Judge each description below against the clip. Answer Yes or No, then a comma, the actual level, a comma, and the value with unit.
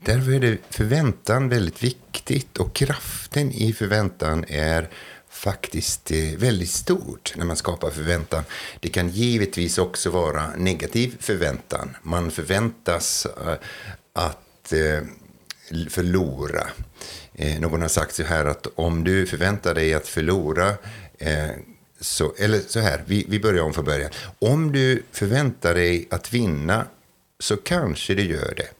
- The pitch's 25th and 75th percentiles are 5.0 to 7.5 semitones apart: Yes, wide, 5.5 semitones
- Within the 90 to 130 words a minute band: Yes, slow, 125 wpm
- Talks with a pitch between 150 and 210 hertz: No, very low, 90 Hz